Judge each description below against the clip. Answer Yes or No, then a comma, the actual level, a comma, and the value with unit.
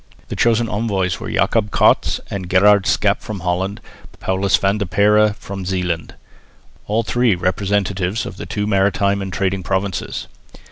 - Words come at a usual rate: Yes, average, 150 wpm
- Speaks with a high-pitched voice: No, low, 100 Hz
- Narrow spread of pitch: Yes, narrow, 1.8 semitones